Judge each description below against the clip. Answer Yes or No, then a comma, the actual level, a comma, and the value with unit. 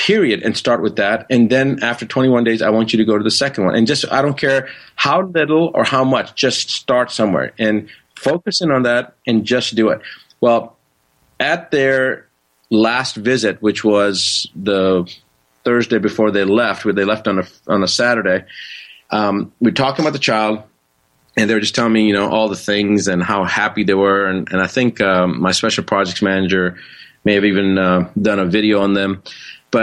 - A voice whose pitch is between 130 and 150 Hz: No, low, 110 Hz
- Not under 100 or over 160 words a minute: No, average, 200 wpm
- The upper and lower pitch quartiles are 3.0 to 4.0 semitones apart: Yes, average, 3.5 semitones